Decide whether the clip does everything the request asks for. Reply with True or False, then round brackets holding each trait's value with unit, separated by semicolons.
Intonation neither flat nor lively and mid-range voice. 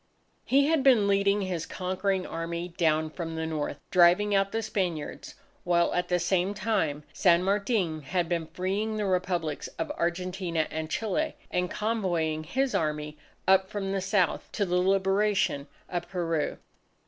True (3.1 semitones; 180 Hz)